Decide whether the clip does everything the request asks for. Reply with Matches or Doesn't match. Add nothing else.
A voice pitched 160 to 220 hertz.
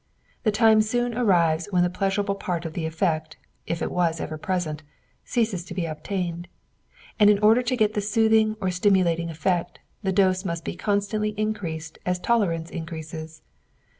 Matches